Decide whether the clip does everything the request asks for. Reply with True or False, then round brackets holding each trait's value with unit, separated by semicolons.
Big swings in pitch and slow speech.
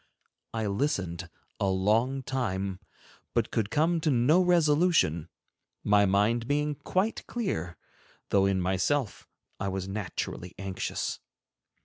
True (7.4 semitones; 115 wpm)